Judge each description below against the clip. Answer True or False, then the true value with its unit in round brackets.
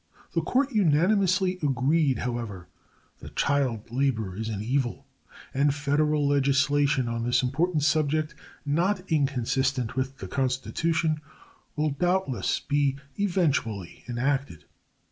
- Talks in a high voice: False (140 Hz)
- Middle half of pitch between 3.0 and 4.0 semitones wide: True (3.6 semitones)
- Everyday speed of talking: False (110 wpm)